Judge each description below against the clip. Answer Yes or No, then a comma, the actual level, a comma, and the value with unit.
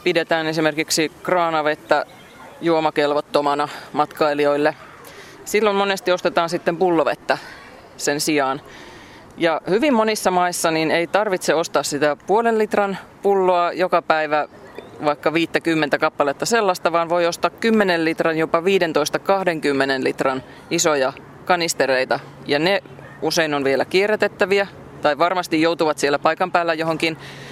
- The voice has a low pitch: No, medium, 165 Hz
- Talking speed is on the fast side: No, average, 115 wpm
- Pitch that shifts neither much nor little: Yes, average, 3.2 semitones